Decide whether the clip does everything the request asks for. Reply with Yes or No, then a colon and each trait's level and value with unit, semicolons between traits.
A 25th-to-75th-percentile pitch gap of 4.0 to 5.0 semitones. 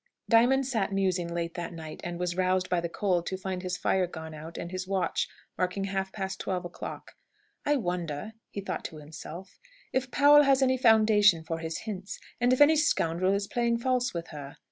Yes: average, 4.5 semitones